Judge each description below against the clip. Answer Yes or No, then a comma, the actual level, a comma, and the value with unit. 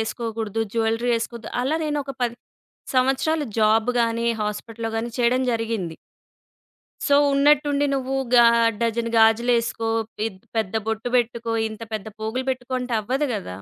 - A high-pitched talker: Yes, high, 235 Hz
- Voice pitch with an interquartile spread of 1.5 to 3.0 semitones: Yes, narrow, 2.4 semitones